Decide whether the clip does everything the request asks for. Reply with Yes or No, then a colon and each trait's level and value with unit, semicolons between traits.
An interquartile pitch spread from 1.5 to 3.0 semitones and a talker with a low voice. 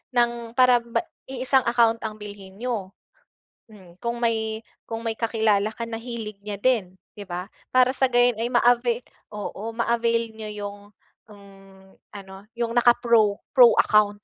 No: narrow, 2.6 semitones; high, 225 Hz